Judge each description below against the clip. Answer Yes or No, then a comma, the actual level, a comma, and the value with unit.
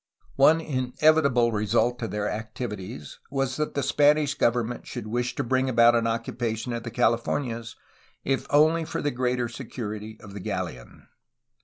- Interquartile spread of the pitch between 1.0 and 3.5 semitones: Yes, average, 3.0 semitones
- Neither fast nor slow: Yes, average, 160 wpm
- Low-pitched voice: Yes, low, 120 Hz